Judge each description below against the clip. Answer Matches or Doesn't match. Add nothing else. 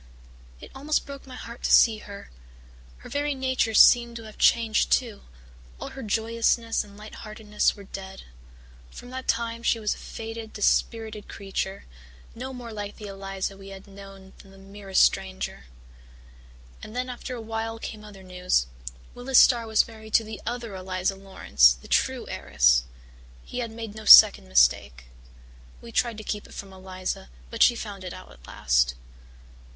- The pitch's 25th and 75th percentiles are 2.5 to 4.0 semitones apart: Matches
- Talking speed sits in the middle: Matches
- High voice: Matches